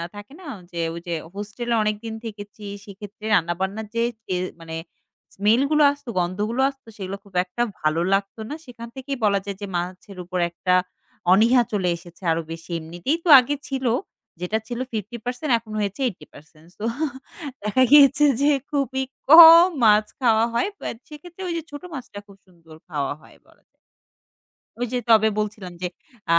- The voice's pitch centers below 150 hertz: No, high, 210 Hz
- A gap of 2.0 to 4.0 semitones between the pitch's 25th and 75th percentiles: No, wide, 5.5 semitones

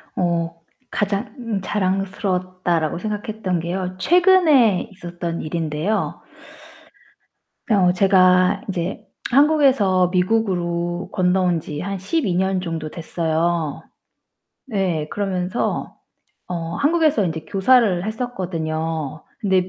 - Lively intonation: No, average, 3.4 semitones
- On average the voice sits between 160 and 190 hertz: Yes, medium, 185 Hz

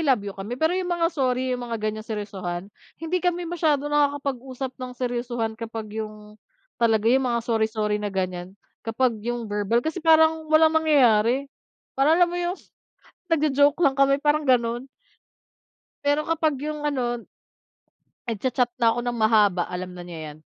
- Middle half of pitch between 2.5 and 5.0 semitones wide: No, wide, 5.5 semitones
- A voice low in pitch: No, very high, 250 Hz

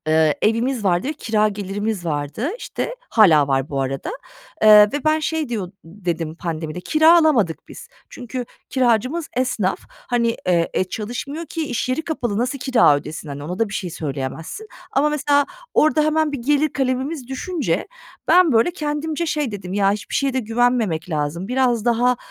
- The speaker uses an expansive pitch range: Yes, wide, 8.1 semitones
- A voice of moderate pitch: No, high, 230 Hz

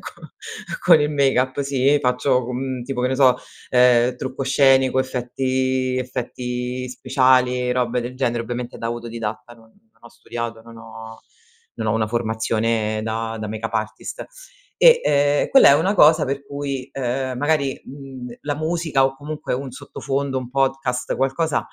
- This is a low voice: Yes, low, 130 Hz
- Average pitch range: No, narrow, 2.3 semitones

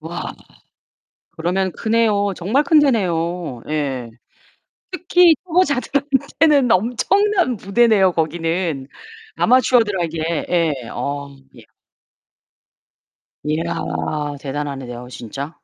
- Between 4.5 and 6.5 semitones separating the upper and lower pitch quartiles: No, wide, 8.2 semitones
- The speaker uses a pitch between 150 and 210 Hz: Yes, medium, 185 Hz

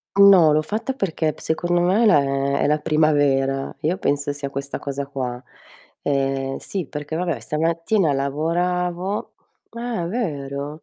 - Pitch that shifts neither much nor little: Yes, average, 4.2 semitones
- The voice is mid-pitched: Yes, medium, 155 Hz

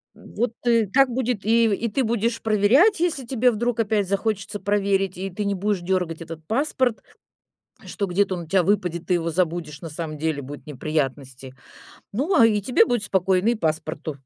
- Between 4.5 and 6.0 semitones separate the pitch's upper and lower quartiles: Yes, average, 5.2 semitones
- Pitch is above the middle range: Yes, high, 200 Hz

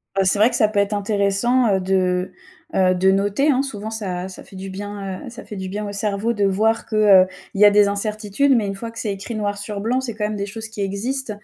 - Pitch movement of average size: No, narrow, 2.1 semitones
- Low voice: No, high, 205 Hz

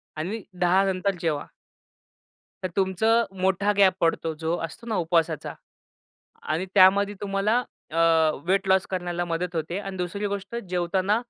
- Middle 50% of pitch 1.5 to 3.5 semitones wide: Yes, narrow, 2.5 semitones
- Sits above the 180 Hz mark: Yes, high, 190 Hz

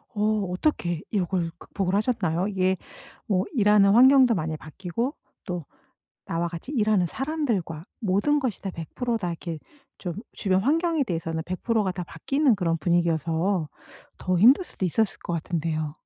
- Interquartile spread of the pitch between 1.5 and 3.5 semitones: No, average, 5.1 semitones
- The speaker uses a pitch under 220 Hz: Yes, high, 190 Hz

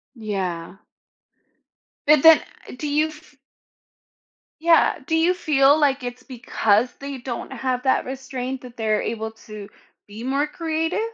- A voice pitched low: No, very high, 265 Hz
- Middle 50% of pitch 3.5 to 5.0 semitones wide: Yes, average, 4.5 semitones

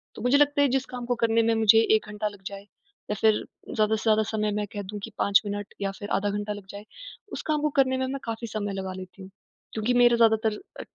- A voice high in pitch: Yes, high, 220 Hz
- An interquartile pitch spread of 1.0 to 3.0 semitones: Yes, narrow, 2.6 semitones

